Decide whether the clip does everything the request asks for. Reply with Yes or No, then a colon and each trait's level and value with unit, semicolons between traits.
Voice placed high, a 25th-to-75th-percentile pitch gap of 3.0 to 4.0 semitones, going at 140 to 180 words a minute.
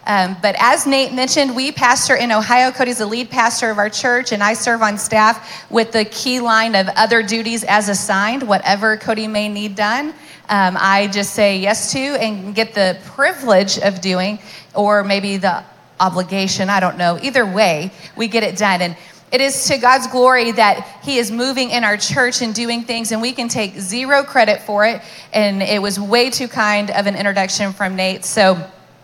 No: high, 215 Hz; average, 3.5 semitones; average, 200 wpm